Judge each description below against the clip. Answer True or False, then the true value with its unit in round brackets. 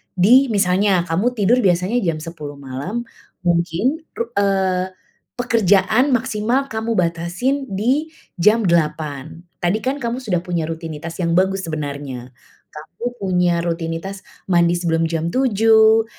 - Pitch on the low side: False (185 Hz)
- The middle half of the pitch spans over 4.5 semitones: True (5.1 semitones)